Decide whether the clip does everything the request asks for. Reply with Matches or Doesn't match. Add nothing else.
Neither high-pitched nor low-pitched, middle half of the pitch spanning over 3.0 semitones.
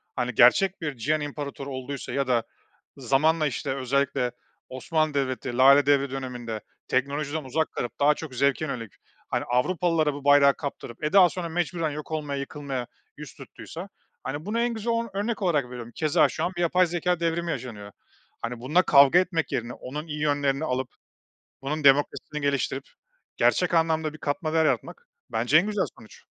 Matches